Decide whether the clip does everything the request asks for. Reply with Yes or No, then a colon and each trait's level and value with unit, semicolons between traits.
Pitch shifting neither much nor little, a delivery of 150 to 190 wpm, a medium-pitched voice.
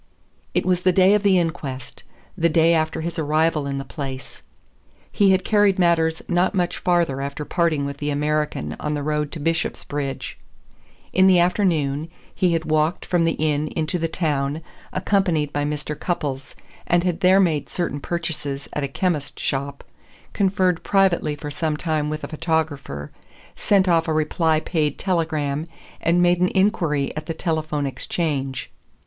Yes: average, 3.1 semitones; average, 165 wpm; medium, 160 Hz